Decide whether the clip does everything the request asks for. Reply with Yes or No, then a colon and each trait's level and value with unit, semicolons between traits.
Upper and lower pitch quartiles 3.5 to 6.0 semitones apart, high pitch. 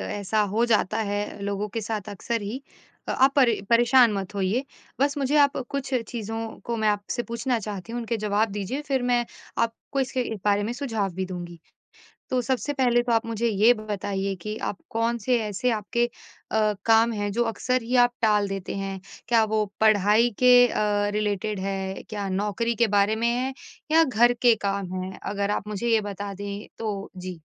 No: average, 3.0 semitones; high, 220 Hz